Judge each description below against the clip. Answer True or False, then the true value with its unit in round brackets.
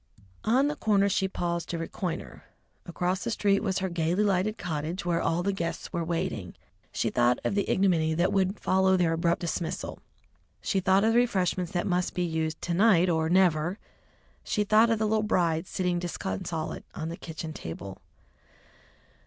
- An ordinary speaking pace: True (175 wpm)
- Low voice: False (180 Hz)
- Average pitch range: True (3.0 semitones)